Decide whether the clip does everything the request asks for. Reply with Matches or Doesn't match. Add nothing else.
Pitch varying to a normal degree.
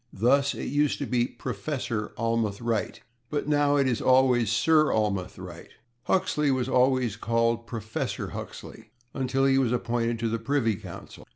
Matches